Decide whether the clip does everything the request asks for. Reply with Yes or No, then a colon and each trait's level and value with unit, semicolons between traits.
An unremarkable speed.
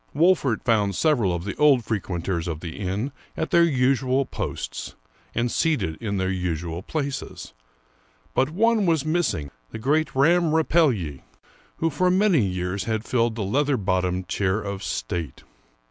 Yes: average, 150 wpm